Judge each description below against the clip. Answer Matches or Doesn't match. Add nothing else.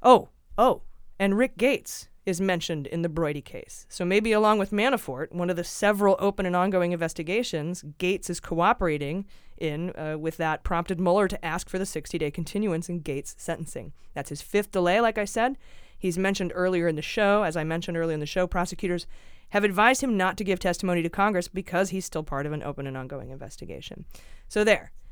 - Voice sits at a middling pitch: Matches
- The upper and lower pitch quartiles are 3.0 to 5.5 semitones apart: Matches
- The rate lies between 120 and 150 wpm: Doesn't match